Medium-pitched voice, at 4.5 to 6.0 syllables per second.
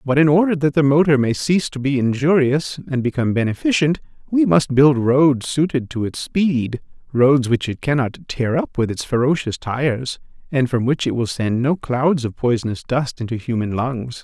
No: low, 130 Hz; 5.0 syllables/s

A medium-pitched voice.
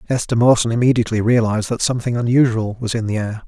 No: low, 115 Hz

